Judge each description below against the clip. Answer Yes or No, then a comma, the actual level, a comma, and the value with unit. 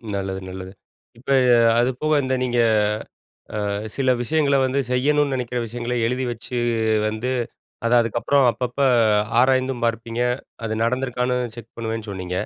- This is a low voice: Yes, low, 125 Hz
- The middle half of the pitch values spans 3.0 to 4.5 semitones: No, narrow, 2.4 semitones